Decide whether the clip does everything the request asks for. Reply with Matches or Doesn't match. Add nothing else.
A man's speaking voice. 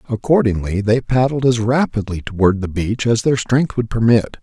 Matches